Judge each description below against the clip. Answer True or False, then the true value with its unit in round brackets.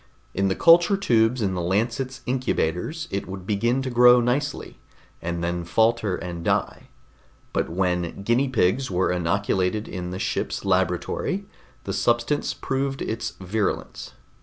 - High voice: False (105 Hz)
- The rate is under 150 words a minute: True (140 wpm)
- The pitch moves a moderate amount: False (5.7 semitones)